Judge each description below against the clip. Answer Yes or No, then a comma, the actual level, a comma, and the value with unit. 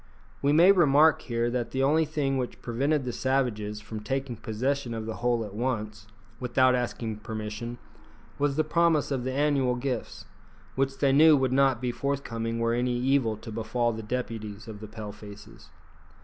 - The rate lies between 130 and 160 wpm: No, average, 175 wpm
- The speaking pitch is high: No, low, 125 Hz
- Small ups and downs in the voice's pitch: No, average, 3.5 semitones